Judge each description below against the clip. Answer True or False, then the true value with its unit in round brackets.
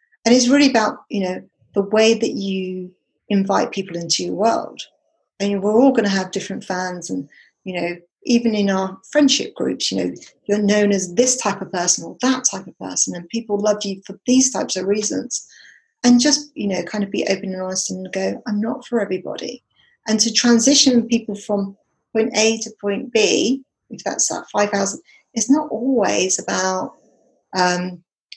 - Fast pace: False (190 wpm)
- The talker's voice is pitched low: False (205 Hz)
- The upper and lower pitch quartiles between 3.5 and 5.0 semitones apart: True (3.9 semitones)